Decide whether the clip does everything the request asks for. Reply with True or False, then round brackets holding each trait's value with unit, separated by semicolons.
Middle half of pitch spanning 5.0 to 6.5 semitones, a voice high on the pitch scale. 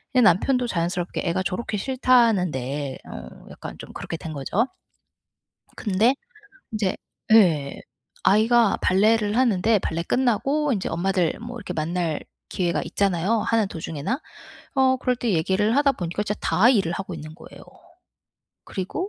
True (5.5 semitones; 200 Hz)